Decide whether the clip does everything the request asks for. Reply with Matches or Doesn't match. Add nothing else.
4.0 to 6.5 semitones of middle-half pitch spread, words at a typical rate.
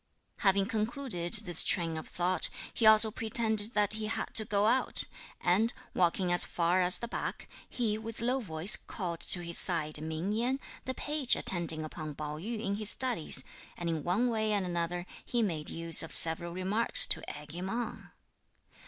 Matches